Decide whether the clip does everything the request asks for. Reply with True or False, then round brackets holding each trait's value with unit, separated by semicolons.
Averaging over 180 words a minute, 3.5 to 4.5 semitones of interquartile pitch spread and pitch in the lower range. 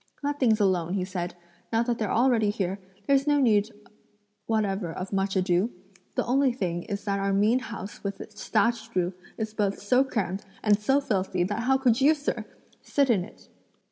False (190 wpm; 3.9 semitones; 210 Hz)